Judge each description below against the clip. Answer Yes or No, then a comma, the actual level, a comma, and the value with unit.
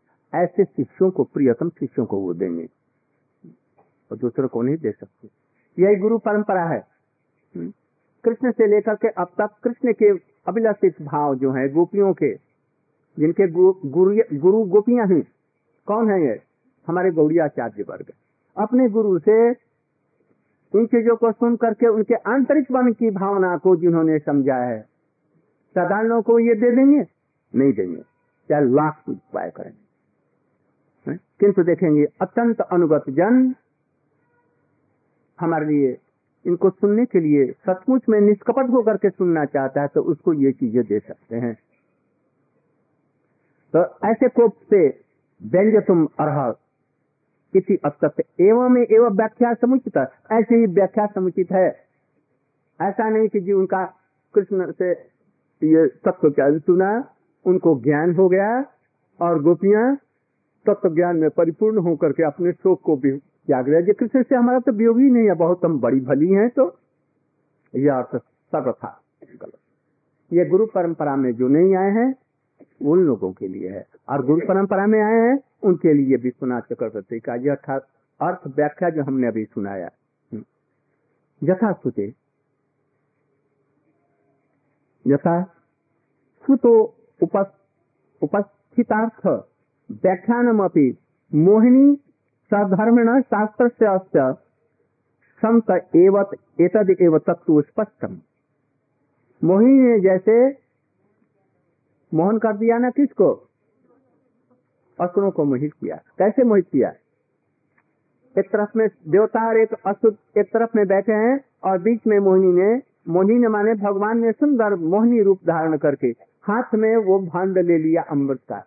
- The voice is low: No, medium, 185 Hz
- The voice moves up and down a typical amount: No, wide, 6.5 semitones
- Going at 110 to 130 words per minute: Yes, average, 120 wpm